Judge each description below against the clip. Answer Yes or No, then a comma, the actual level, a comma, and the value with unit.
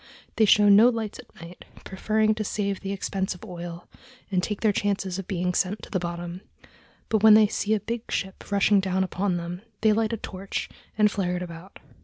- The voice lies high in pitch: Yes, high, 195 Hz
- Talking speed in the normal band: No, fast, 210 wpm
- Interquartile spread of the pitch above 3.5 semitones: No, average, 2.8 semitones